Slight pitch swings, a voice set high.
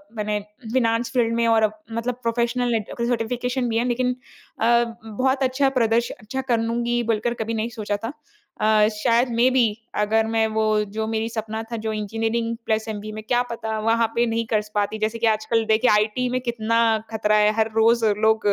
Yes: narrow, 1.6 semitones; high, 225 Hz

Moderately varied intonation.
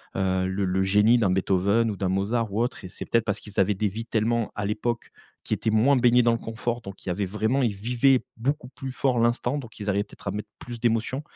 Yes: average, 3.1 semitones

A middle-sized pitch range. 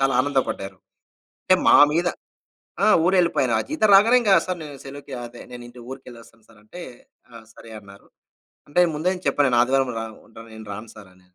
No: wide, 6.6 semitones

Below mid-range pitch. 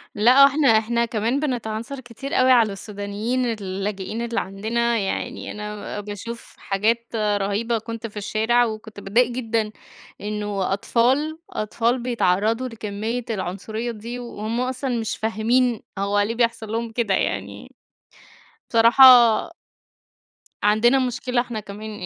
No: high, 225 Hz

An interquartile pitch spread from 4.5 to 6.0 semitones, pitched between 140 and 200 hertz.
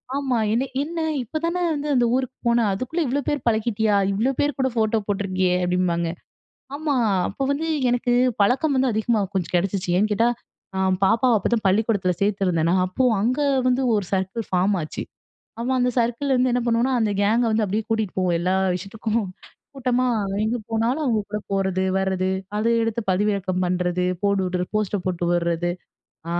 No: average, 4.8 semitones; high, 215 Hz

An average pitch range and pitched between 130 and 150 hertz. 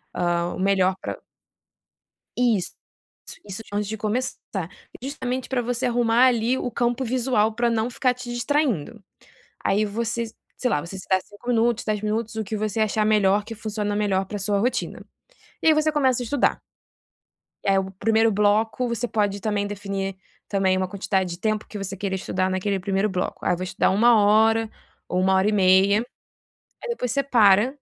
No: average, 3.5 semitones; high, 215 Hz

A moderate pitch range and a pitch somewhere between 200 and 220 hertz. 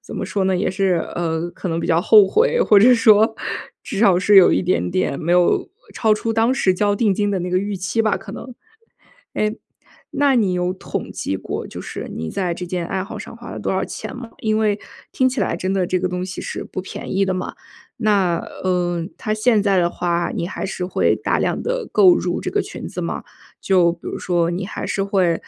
No: average, 3.3 semitones; high, 190 Hz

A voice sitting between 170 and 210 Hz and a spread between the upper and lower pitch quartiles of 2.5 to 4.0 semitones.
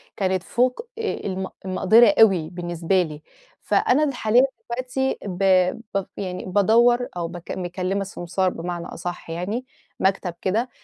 No: high, 190 Hz; average, 5.0 semitones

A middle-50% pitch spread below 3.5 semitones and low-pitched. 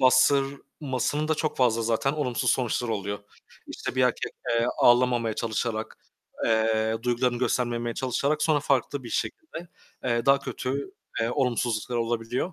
Yes: average, 2.9 semitones; low, 125 Hz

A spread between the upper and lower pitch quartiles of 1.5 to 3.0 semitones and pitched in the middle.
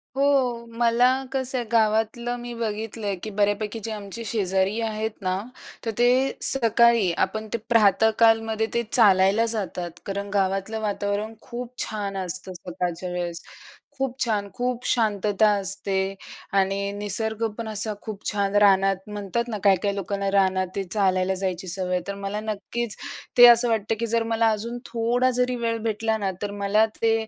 No: average, 2.7 semitones; high, 215 Hz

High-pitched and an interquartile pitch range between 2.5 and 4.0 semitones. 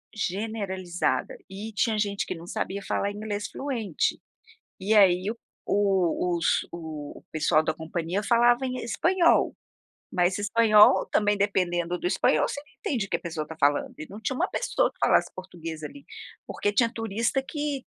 No: high, 200 Hz; average, 4.4 semitones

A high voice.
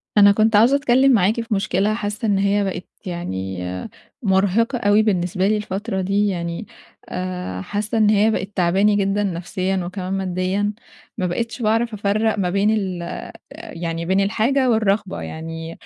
Yes: high, 200 Hz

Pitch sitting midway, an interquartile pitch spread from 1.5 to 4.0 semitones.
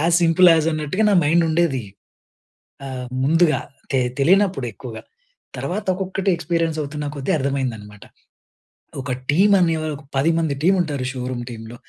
No: medium, 155 Hz; average, 4.4 semitones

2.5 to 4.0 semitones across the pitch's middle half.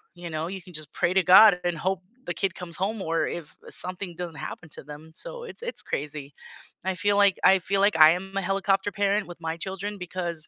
Yes: average, 2.9 semitones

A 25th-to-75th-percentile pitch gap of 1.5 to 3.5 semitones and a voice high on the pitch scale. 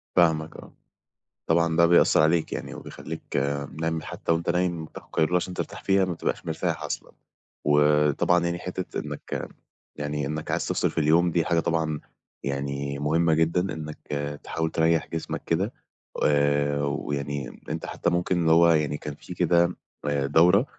No: narrow, 2.5 semitones; very low, 80 Hz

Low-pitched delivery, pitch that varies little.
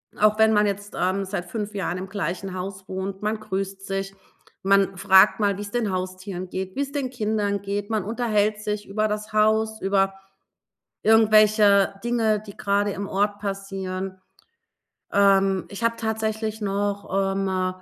No: high, 200 Hz; narrow, 1.8 semitones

